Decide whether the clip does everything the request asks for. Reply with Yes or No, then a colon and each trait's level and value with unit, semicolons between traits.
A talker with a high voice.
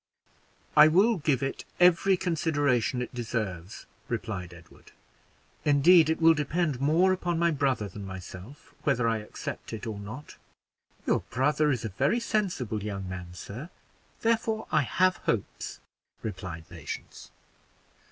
No: low, 135 Hz